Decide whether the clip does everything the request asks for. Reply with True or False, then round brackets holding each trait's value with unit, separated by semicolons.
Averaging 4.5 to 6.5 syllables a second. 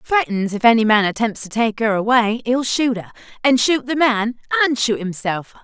True (5.1 syllables/s)